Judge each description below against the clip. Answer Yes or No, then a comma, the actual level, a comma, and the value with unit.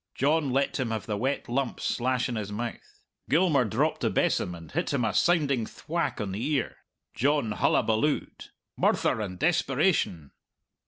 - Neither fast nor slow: Yes, average, 160 wpm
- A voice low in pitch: Yes, low, 125 Hz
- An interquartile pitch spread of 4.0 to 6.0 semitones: Yes, average, 4.9 semitones